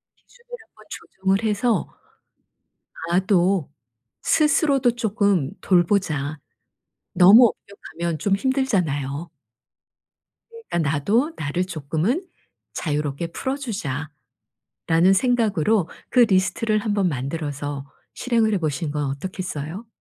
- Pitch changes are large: Yes, wide, 6.6 semitones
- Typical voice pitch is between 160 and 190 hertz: Yes, medium, 185 Hz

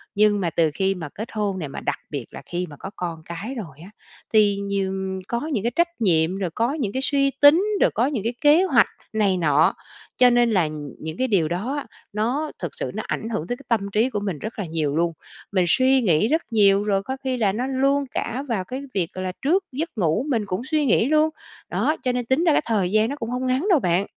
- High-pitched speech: Yes, high, 215 Hz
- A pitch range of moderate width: No, wide, 6.0 semitones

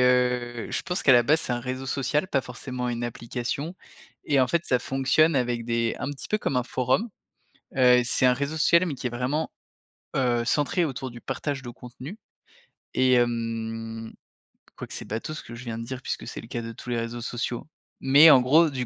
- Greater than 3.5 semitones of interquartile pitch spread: No, narrow, 2.6 semitones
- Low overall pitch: Yes, low, 125 Hz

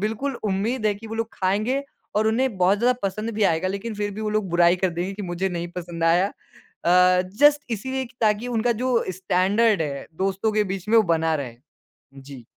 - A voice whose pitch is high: Yes, high, 200 Hz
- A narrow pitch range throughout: No, average, 3.8 semitones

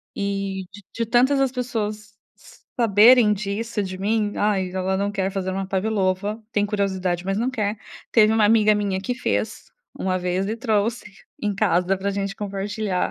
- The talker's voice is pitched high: Yes, high, 205 Hz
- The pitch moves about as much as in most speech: No, narrow, 2.3 semitones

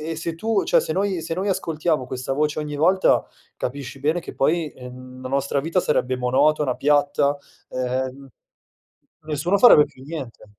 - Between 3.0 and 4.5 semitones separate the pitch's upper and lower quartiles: Yes, average, 4.0 semitones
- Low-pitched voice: No, medium, 150 Hz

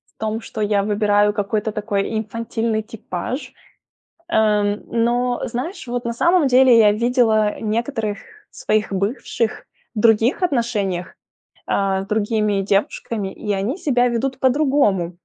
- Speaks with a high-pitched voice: Yes, high, 220 Hz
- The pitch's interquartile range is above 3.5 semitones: No, average, 2.8 semitones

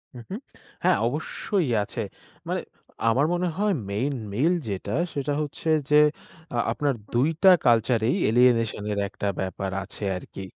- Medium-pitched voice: No, low, 120 Hz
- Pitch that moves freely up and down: Yes, wide, 5.7 semitones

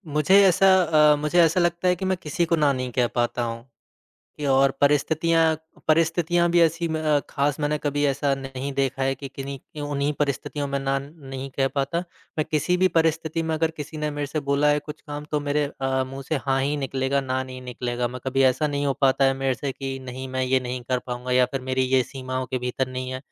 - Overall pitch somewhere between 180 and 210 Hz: No, medium, 140 Hz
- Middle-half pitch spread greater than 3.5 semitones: No, average, 2.7 semitones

